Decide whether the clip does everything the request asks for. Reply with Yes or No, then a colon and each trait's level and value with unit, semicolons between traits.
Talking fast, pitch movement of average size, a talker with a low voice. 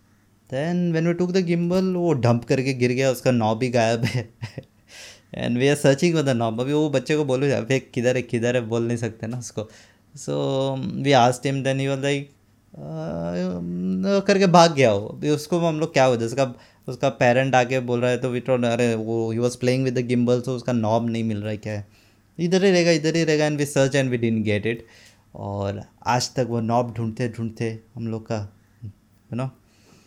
Yes: fast, 220 wpm; average, 3.6 semitones; low, 125 Hz